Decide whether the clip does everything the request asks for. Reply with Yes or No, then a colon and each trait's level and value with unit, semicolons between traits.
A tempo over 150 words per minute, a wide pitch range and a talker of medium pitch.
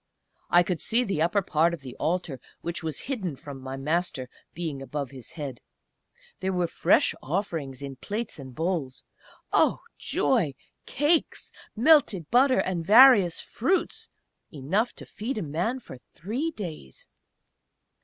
No: average, 145 wpm; wide, 7.2 semitones; medium, 170 Hz